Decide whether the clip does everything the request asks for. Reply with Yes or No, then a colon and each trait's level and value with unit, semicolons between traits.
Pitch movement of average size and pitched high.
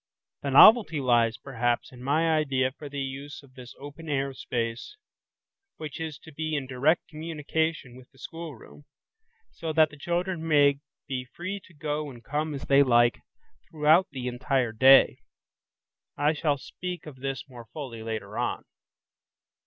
No: average, 3.5 semitones; medium, 140 Hz